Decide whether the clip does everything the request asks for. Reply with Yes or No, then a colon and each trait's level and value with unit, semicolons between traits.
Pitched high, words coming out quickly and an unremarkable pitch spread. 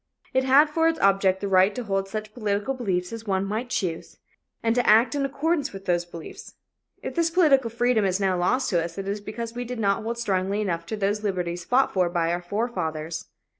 Yes: high, 205 Hz; fast, 220 wpm; average, 4.8 semitones